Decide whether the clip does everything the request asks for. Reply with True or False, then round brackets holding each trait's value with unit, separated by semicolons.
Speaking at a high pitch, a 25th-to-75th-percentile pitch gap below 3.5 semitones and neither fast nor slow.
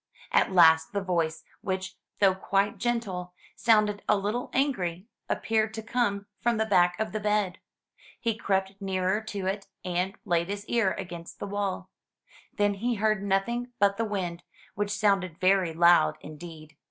True (195 Hz; 2.9 semitones; 160 wpm)